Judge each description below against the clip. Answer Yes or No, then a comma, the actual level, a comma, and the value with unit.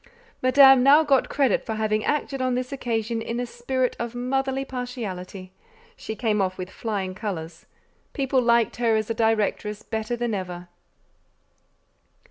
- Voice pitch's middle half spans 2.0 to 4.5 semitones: Yes, average, 3.4 semitones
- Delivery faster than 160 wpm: No, average, 150 wpm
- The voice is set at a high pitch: Yes, high, 235 Hz